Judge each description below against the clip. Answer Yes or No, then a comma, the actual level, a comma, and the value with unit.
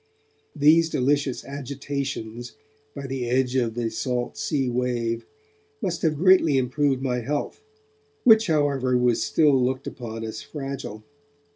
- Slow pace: Yes, slow, 130 wpm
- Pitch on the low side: Yes, low, 130 Hz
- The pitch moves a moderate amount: Yes, average, 3.0 semitones